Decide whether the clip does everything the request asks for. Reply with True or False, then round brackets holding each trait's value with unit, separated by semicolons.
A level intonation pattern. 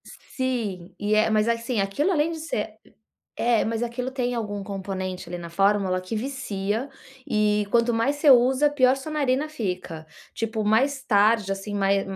False (4.6 semitones)